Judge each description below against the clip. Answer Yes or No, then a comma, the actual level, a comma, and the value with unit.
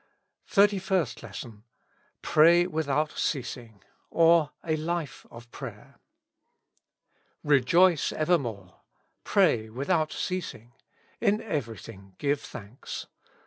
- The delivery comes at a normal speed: No, slow, 95 wpm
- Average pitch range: No, wide, 6.5 semitones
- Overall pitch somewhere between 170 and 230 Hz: No, medium, 150 Hz